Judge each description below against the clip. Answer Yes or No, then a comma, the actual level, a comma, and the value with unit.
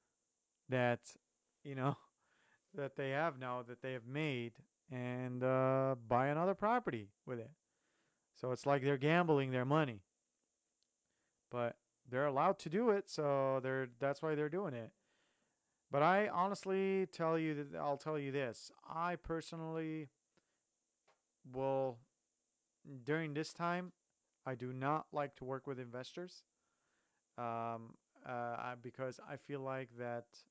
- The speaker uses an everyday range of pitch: Yes, average, 4.0 semitones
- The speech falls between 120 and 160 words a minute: Yes, average, 140 wpm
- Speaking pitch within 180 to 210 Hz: No, low, 135 Hz